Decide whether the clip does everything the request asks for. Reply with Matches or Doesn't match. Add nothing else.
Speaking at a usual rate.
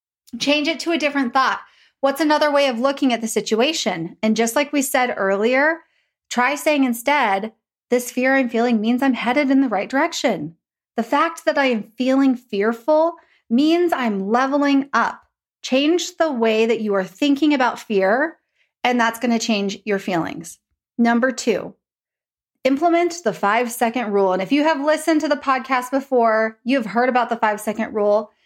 Matches